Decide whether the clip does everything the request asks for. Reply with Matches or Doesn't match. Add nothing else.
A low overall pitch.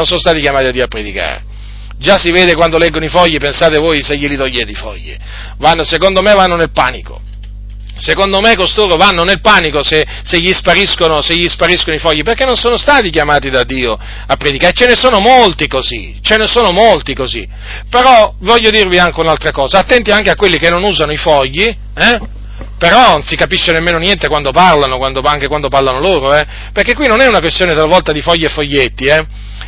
Doesn't match